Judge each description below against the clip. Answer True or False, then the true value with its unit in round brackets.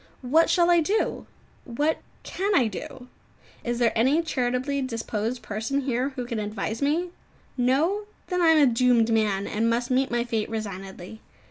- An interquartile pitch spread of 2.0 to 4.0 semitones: False (4.5 semitones)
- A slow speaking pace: False (165 wpm)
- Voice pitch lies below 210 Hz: False (245 Hz)